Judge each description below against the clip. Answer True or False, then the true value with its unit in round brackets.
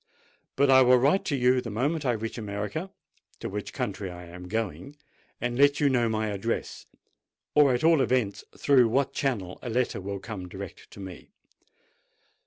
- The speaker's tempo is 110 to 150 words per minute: False (170 wpm)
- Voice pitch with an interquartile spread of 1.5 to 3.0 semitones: False (5.3 semitones)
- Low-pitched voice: True (120 Hz)